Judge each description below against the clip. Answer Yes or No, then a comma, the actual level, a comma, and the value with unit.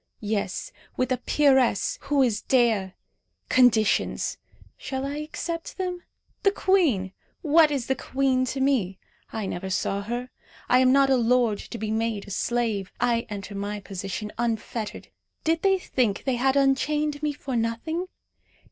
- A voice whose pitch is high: Yes, very high, 250 Hz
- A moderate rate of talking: Yes, average, 155 wpm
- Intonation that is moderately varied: Yes, average, 4.7 semitones